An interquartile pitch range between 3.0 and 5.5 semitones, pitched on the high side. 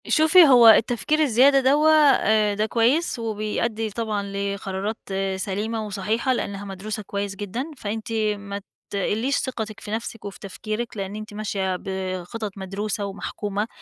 No: narrow, 2.5 semitones; high, 215 Hz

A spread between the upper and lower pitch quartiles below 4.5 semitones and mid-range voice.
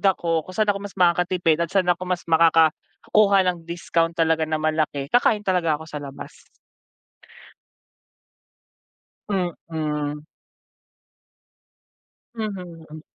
Yes: narrow, 2.6 semitones; medium, 170 Hz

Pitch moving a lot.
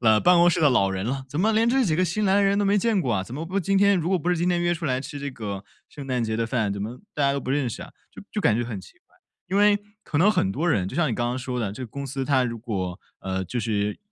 Yes: wide, 7.8 semitones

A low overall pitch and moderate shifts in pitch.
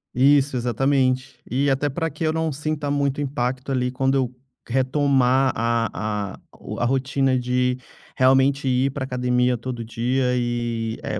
No: low, 130 Hz; narrow, 1.9 semitones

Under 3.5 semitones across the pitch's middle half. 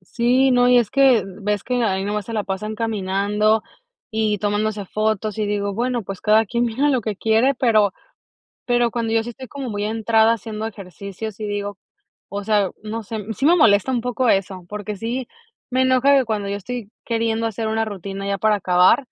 Yes: average, 2.7 semitones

